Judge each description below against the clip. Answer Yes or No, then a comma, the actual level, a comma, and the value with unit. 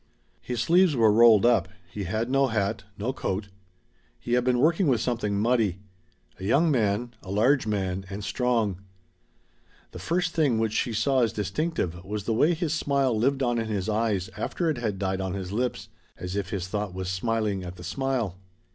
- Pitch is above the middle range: No, low, 110 Hz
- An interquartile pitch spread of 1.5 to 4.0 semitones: No, average, 4.6 semitones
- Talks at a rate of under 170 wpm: No, average, 190 wpm